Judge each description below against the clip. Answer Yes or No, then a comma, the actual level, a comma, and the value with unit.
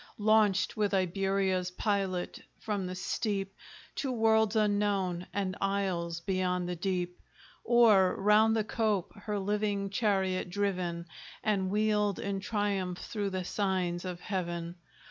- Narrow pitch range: Yes, narrow, 2.2 semitones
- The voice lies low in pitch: No, high, 195 Hz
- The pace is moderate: No, slow, 125 wpm